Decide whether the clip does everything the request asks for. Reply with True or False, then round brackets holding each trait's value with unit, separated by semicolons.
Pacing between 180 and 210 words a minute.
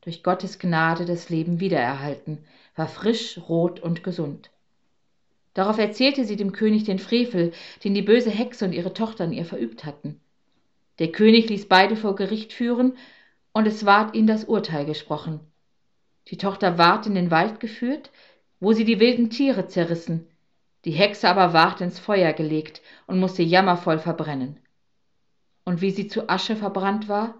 False (160 wpm)